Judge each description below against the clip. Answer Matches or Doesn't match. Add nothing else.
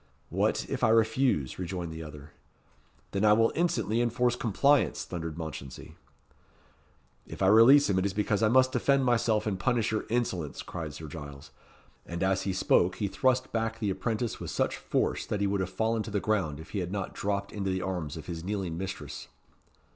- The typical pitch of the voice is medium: Doesn't match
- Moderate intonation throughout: Matches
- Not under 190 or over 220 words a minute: Matches